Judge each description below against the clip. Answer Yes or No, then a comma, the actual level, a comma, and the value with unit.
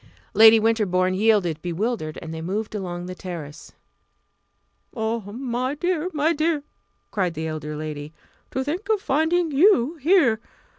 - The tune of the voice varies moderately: No, wide, 9.0 semitones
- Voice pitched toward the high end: Yes, high, 220 Hz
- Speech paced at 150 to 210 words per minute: No, average, 140 wpm